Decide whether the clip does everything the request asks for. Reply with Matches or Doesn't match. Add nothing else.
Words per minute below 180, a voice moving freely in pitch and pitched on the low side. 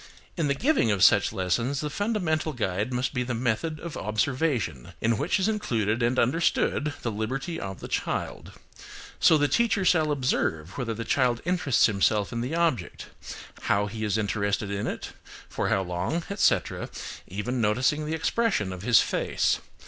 Matches